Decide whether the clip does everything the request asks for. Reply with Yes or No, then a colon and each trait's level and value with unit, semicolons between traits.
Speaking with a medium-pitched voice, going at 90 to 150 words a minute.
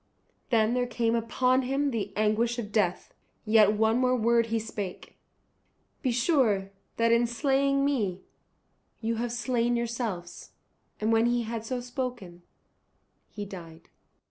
No: high, 230 Hz; average, 140 wpm